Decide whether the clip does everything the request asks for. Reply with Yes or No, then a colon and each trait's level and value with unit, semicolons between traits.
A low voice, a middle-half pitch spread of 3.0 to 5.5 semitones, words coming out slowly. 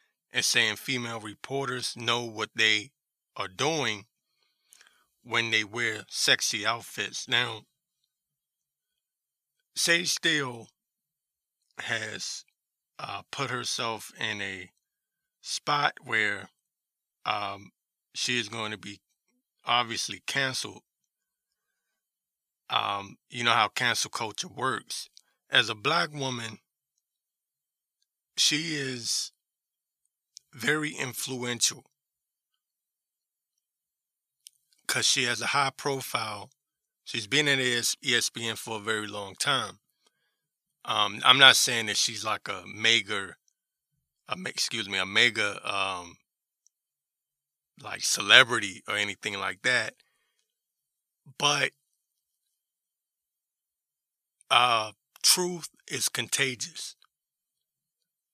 Yes: low, 130 Hz; average, 5.0 semitones; slow, 90 wpm